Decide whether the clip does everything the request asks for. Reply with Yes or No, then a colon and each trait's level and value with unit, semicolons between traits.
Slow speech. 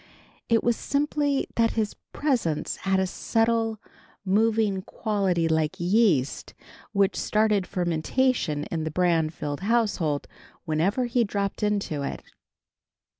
Yes: slow, 115 wpm